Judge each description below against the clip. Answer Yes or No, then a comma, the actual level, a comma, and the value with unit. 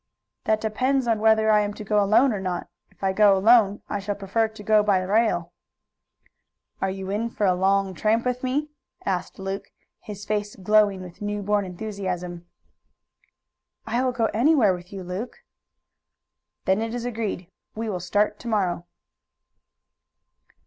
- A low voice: No, high, 205 Hz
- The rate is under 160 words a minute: No, average, 165 wpm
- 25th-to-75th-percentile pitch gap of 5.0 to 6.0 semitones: No, narrow, 2.6 semitones